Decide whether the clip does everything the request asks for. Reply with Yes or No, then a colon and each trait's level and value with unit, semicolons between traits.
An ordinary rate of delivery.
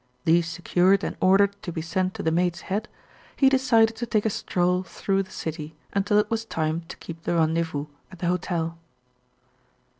Yes: average, 185 wpm